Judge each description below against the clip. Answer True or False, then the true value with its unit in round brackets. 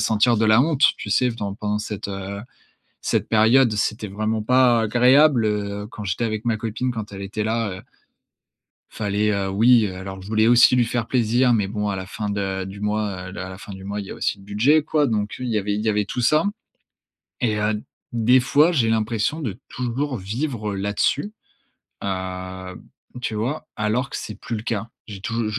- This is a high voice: False (110 Hz)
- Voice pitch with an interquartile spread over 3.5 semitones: False (3.0 semitones)